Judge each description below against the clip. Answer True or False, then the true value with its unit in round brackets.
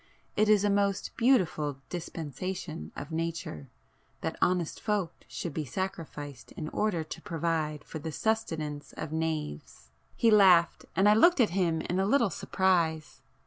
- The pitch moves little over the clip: False (4.2 semitones)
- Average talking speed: True (145 wpm)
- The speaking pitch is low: False (170 Hz)